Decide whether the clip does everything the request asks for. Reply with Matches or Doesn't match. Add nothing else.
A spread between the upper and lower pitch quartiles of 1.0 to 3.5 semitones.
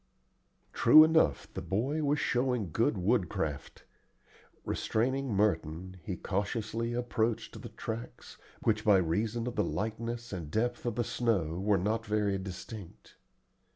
Doesn't match